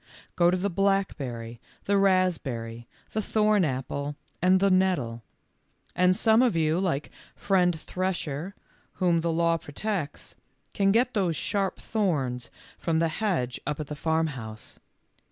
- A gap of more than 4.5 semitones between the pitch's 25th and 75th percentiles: Yes, average, 5.2 semitones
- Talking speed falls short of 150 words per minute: Yes, slow, 135 wpm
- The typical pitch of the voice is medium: Yes, medium, 170 Hz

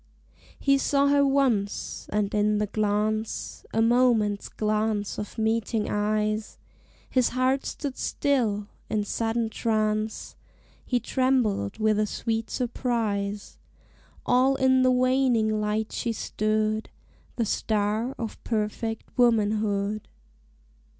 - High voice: Yes, high, 220 Hz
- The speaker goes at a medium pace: No, slow, 110 wpm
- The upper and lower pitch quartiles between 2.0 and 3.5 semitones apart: Yes, average, 2.8 semitones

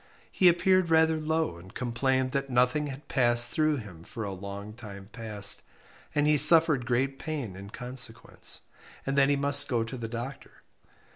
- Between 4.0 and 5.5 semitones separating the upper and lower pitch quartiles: Yes, average, 4.7 semitones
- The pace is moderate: Yes, average, 170 wpm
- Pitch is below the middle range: Yes, low, 130 Hz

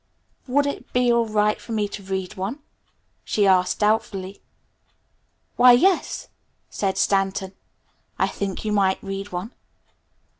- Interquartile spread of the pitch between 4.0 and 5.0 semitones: No, average, 3.2 semitones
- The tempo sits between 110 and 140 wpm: Yes, slow, 135 wpm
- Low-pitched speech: No, high, 205 Hz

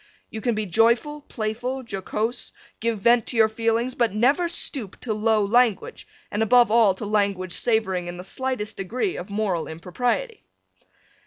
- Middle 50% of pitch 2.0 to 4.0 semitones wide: Yes, average, 3.3 semitones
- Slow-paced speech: No, average, 160 wpm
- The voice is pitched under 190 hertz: No, high, 220 Hz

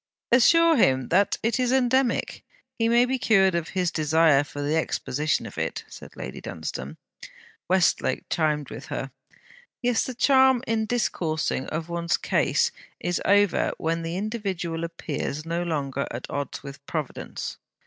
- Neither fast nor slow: Yes, average, 150 wpm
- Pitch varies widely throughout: Yes, wide, 6.8 semitones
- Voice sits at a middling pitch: Yes, medium, 170 Hz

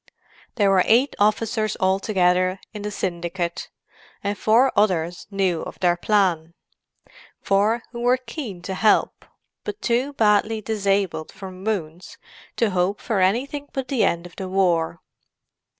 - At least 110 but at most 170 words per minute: Yes, slow, 135 wpm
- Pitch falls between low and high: No, high, 195 Hz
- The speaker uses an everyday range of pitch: Yes, average, 3.4 semitones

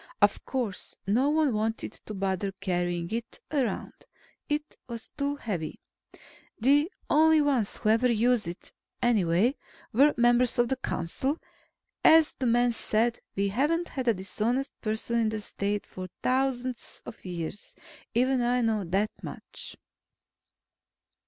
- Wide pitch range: No, average, 4.5 semitones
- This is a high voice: Yes, high, 235 Hz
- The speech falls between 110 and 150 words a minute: Yes, average, 140 wpm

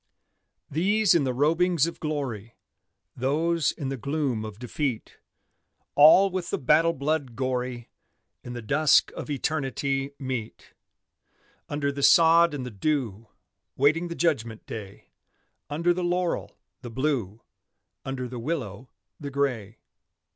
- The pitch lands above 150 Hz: No, medium, 140 Hz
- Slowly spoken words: Yes, slow, 130 wpm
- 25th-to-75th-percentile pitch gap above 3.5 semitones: Yes, average, 4.5 semitones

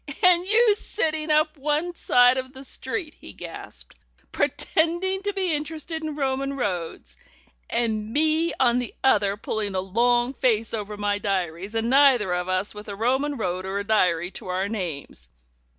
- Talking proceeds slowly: No, average, 165 wpm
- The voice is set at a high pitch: Yes, high, 245 Hz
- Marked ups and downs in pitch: Yes, wide, 7.3 semitones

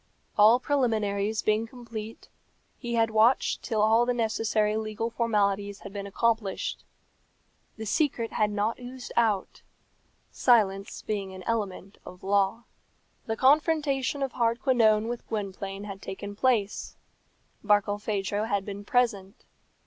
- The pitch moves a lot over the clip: No, narrow, 2.6 semitones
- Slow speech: Yes, slow, 125 wpm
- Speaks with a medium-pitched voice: No, high, 215 Hz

